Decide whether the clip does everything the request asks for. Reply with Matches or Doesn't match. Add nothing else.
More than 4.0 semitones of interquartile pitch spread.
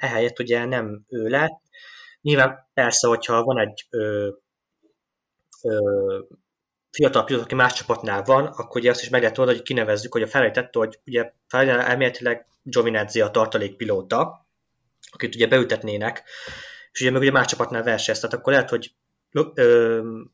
Doesn't match